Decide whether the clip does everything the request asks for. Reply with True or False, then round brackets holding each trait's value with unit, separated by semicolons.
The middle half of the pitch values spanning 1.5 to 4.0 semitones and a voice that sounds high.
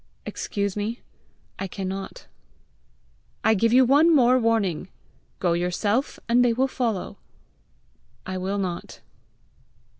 False (4.4 semitones; 215 Hz)